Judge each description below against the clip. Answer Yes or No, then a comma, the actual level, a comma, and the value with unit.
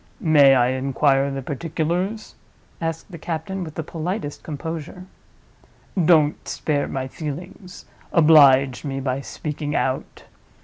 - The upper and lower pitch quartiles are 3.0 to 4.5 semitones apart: Yes, average, 3.5 semitones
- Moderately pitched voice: Yes, medium, 150 Hz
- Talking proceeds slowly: Yes, slow, 120 wpm